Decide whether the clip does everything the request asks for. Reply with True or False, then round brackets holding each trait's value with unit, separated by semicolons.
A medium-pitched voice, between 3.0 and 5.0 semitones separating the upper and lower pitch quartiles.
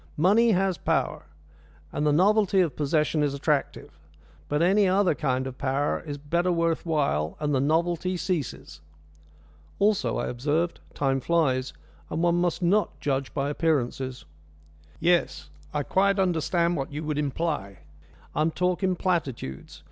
True (160 Hz; 4.2 semitones)